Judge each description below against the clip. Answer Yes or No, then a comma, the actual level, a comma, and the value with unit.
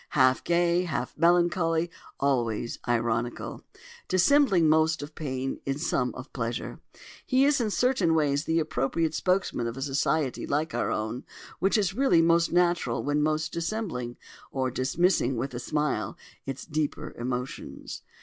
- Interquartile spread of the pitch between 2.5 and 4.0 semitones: No, average, 5.0 semitones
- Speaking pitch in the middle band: Yes, medium, 155 Hz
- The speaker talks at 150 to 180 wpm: No, average, 140 wpm